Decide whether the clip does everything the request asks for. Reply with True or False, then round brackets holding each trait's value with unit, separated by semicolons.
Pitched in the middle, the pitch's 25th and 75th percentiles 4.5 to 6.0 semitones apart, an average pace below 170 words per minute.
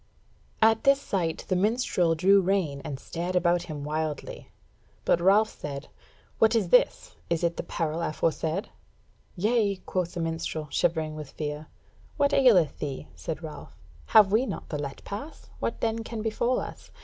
True (175 Hz; 5.5 semitones; 160 wpm)